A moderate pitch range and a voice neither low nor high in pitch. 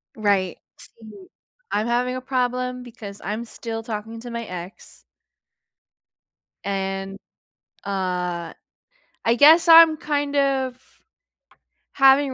No: average, 5.0 semitones; high, 235 Hz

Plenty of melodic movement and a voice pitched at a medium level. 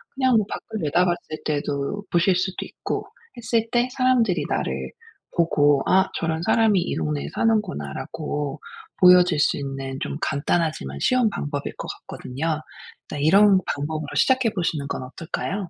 Yes: wide, 6.2 semitones; medium, 165 Hz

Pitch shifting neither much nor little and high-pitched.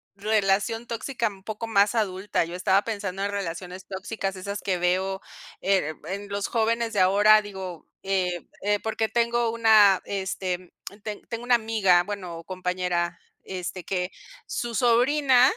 Yes: average, 3.2 semitones; high, 200 Hz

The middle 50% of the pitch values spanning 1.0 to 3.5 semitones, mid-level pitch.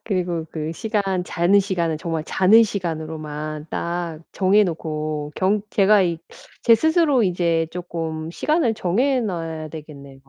No: average, 4.2 semitones; medium, 175 Hz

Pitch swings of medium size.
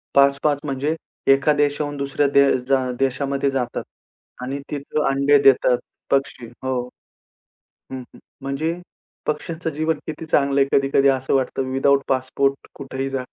No: narrow, 1.4 semitones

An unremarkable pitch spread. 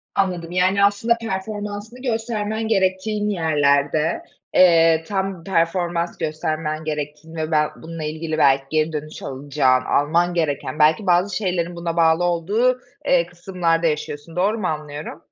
Yes: average, 3.8 semitones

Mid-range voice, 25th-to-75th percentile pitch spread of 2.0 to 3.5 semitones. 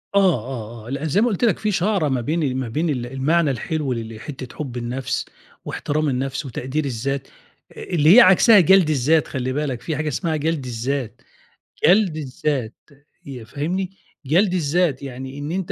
No: medium, 145 Hz; average, 4.5 semitones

